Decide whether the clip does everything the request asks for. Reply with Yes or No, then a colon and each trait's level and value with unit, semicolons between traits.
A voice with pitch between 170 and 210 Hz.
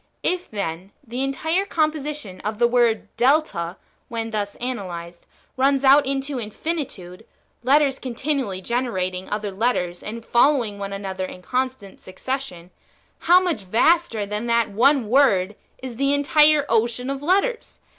No: high, 240 Hz